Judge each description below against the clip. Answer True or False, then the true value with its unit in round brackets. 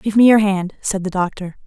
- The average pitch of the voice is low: False (195 Hz)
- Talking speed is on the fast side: True (250 wpm)